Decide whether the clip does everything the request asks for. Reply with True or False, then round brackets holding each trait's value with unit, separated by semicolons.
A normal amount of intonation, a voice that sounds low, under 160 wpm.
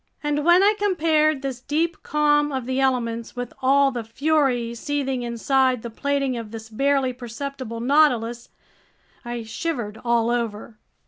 False (3.7 semitones; 260 Hz; 145 wpm)